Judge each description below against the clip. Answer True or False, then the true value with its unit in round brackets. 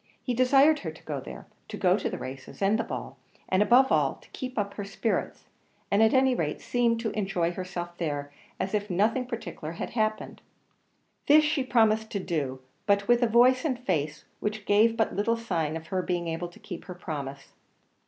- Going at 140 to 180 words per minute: False (200 wpm)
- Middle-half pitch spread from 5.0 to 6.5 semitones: True (5.5 semitones)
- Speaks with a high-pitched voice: True (205 Hz)